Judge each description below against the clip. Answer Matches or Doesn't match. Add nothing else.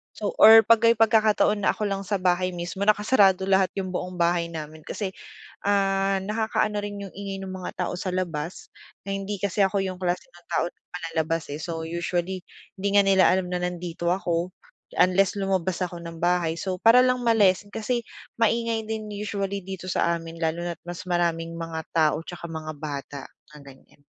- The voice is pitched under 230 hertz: Matches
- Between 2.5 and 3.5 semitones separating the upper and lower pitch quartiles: Matches